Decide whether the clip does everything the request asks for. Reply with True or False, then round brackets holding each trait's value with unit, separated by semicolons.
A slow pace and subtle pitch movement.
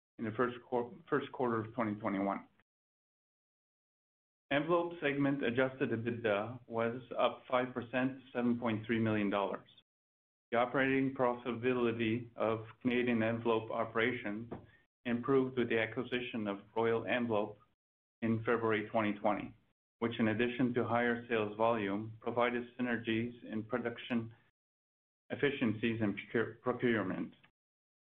True (100 wpm; 2.0 semitones)